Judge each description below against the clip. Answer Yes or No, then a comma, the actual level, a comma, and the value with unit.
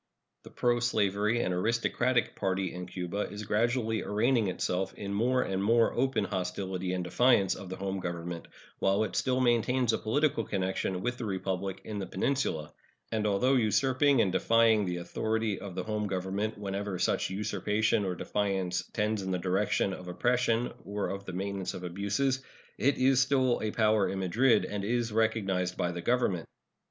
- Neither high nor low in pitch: No, low, 105 Hz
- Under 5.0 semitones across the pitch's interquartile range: Yes, average, 3.6 semitones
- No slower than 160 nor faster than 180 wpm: Yes, average, 170 wpm